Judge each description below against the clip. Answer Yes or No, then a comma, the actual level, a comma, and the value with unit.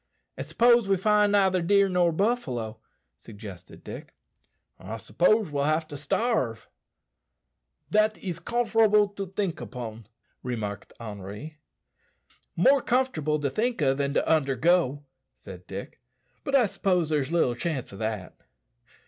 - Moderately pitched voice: Yes, medium, 160 Hz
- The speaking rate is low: Yes, slow, 130 wpm